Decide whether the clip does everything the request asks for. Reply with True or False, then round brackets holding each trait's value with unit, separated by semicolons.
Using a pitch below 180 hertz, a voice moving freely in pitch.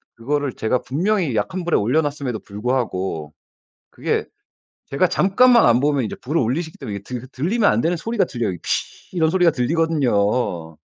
True (135 Hz; 6.5 semitones)